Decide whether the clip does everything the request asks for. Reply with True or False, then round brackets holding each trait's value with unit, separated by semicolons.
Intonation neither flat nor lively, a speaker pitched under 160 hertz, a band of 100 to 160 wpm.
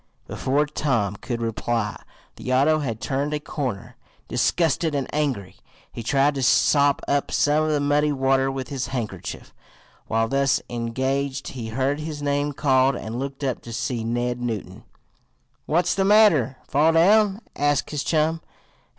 True (3.4 semitones; 135 Hz; 155 wpm)